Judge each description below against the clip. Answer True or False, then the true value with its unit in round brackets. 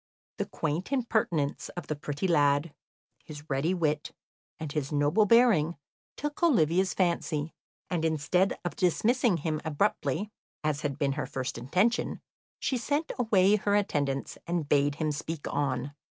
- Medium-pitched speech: True (160 Hz)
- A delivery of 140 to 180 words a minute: True (145 wpm)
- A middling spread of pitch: True (5.0 semitones)